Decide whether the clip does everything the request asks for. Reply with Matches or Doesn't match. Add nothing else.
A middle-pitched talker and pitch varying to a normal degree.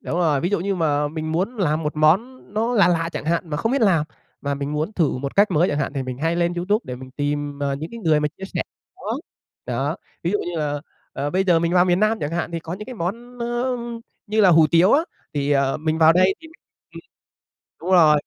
Matches